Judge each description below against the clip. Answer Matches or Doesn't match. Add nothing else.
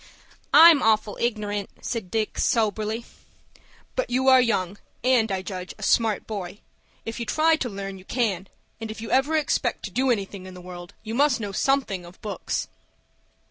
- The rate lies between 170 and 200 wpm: Matches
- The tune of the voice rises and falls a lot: Doesn't match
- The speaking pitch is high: Matches